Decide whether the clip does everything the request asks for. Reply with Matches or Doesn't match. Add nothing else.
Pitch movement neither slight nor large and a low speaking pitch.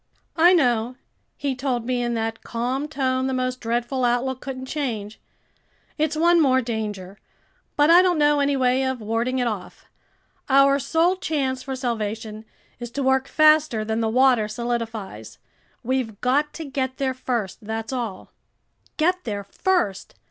Doesn't match